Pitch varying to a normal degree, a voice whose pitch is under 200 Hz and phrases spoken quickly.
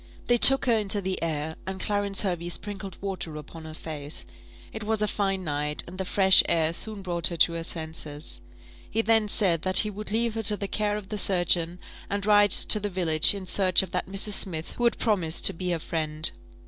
Yes: average, 3.9 semitones; high, 190 Hz; fast, 220 wpm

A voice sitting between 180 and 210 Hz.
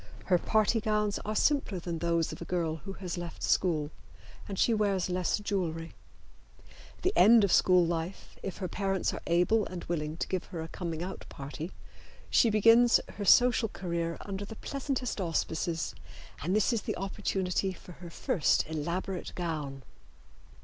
Yes: medium, 185 Hz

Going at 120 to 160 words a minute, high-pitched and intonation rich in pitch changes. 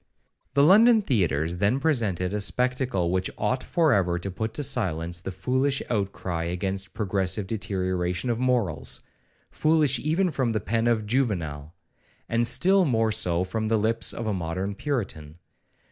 No: average, 150 wpm; low, 105 Hz; wide, 5.8 semitones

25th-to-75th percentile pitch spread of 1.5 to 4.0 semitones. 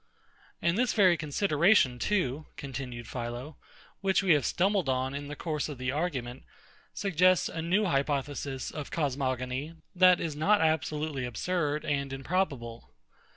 No: average, 5.0 semitones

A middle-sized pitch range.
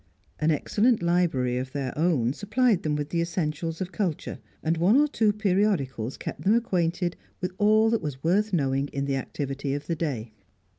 No: wide, 6.4 semitones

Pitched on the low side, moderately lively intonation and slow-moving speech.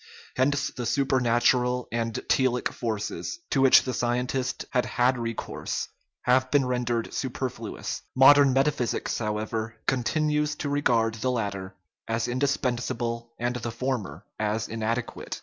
No: low, 125 Hz; narrow, 2.3 semitones; slow, 130 wpm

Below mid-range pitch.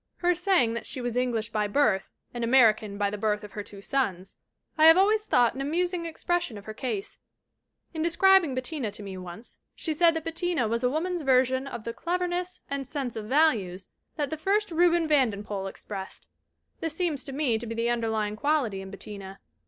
No: very high, 255 Hz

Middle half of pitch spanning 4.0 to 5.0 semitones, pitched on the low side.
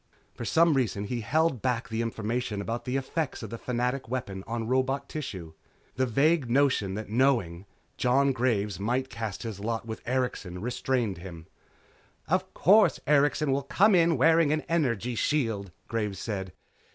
Yes: average, 4.4 semitones; low, 125 Hz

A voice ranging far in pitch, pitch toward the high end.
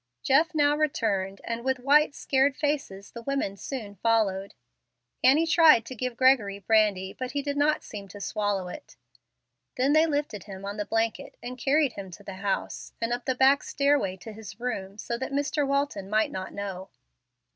Yes: wide, 5.7 semitones; high, 235 Hz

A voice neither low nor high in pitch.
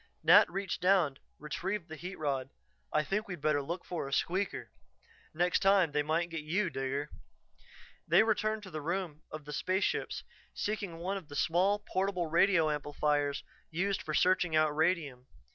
Yes: medium, 170 Hz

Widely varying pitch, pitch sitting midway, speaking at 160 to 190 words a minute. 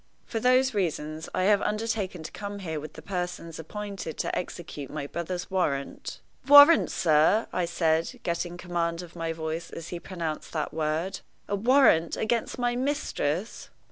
No: average, 4.5 semitones; medium, 175 Hz; average, 165 wpm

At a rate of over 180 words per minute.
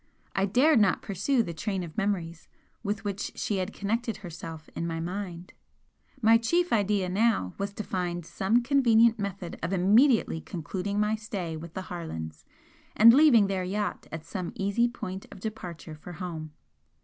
No: average, 165 wpm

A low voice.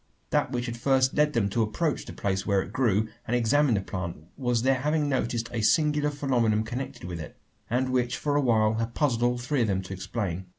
Yes: low, 120 Hz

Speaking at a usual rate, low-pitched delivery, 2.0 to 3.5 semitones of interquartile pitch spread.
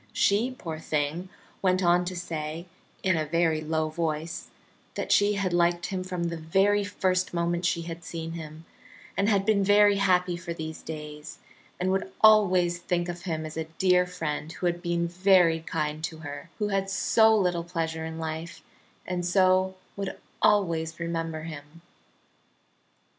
No: average, 165 wpm; medium, 175 Hz; narrow, 2.6 semitones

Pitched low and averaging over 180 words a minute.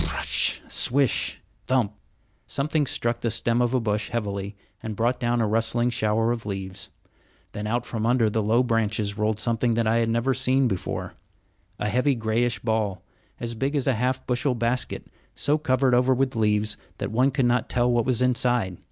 Yes: low, 115 Hz; average, 195 wpm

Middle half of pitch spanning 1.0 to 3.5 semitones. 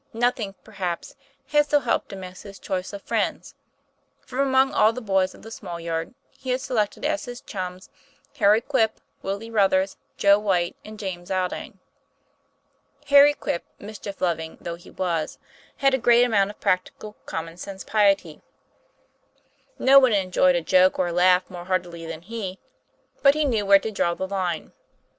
No: average, 4.0 semitones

